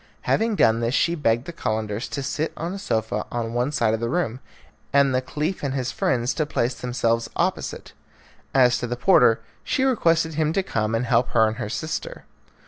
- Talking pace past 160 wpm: Yes, fast, 205 wpm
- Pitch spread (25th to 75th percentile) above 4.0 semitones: Yes, wide, 5.4 semitones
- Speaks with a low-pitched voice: Yes, low, 125 Hz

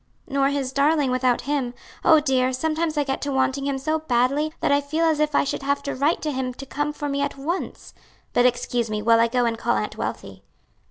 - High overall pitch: Yes, very high, 280 Hz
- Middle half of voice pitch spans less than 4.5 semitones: Yes, average, 2.7 semitones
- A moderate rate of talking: No, fast, 235 wpm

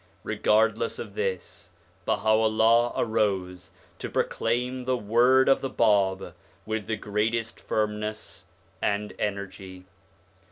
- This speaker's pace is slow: Yes, slow, 105 wpm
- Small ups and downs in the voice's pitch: Yes, narrow, 2.2 semitones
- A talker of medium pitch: No, low, 110 Hz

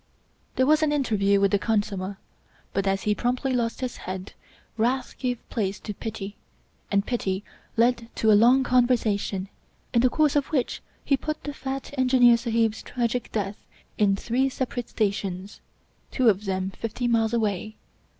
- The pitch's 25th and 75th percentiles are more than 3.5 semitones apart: Yes, average, 4.0 semitones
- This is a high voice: Yes, high, 230 Hz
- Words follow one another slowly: No, average, 165 wpm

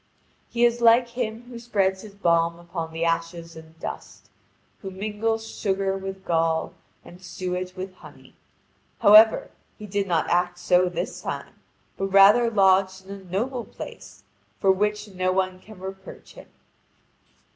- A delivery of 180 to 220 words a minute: No, average, 150 wpm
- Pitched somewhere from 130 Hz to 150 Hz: No, high, 190 Hz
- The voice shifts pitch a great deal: No, average, 2.9 semitones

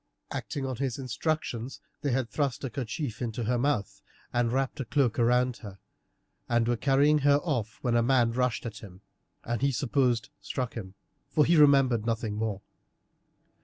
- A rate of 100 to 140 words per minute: No, average, 170 wpm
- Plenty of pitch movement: No, average, 3.1 semitones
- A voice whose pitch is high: No, low, 125 Hz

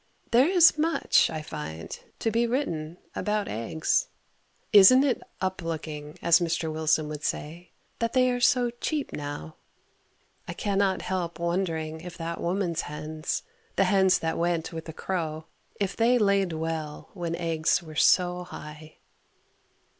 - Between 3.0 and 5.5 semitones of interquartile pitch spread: Yes, average, 4.1 semitones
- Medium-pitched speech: Yes, medium, 170 Hz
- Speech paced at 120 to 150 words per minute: Yes, average, 145 wpm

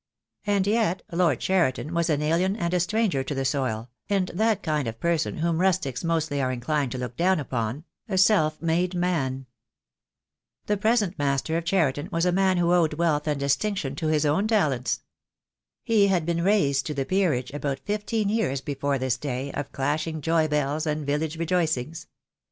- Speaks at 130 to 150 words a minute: No, average, 185 wpm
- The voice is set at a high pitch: No, medium, 160 Hz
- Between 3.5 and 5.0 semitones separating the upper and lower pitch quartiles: Yes, average, 4.6 semitones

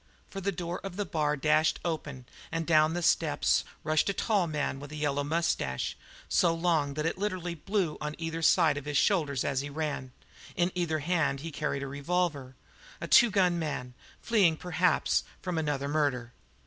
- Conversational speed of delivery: Yes, average, 185 wpm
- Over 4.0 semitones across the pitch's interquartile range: No, average, 3.4 semitones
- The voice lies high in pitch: No, medium, 155 Hz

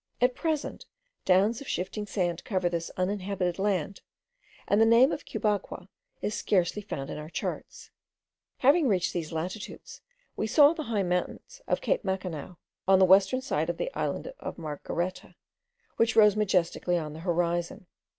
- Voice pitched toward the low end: No, high, 190 Hz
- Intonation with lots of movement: No, average, 3.9 semitones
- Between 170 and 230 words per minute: No, average, 160 wpm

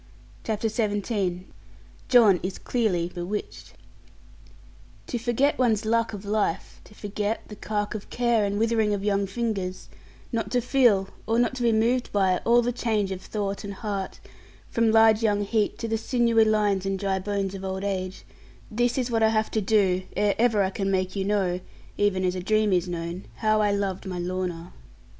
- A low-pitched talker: No, high, 205 Hz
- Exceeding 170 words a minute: Yes, average, 185 wpm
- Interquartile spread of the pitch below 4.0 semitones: Yes, average, 2.7 semitones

